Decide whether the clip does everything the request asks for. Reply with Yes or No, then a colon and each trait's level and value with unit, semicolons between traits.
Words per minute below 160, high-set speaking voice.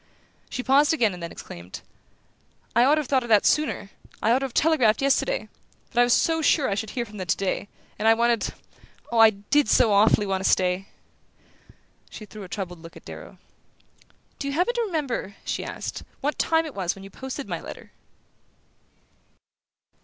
No: average, 190 wpm; high, 230 Hz